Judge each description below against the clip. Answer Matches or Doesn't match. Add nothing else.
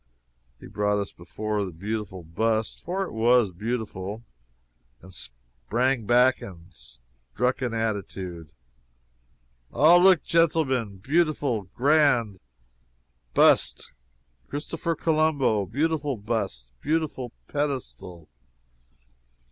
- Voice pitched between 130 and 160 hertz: Doesn't match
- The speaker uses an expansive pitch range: Matches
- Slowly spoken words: Matches